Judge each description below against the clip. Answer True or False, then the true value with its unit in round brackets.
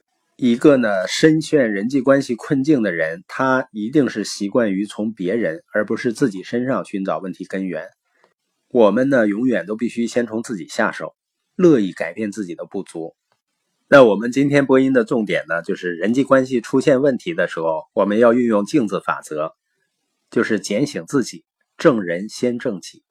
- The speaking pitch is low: True (120 Hz)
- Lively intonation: False (4.0 semitones)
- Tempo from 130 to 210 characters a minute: False (270 characters per minute)